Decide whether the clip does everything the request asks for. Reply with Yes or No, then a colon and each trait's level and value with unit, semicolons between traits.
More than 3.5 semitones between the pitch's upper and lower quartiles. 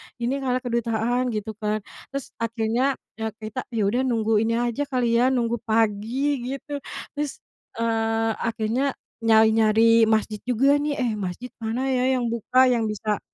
No: narrow, 2.5 semitones